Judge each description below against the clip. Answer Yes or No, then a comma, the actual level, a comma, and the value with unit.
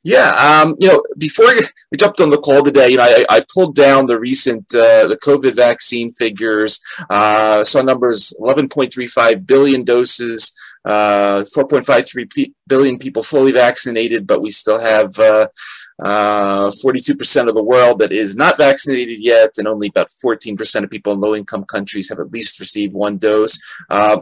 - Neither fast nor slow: Yes, average, 170 wpm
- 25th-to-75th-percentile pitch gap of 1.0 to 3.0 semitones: No, average, 4.0 semitones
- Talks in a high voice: No, low, 120 Hz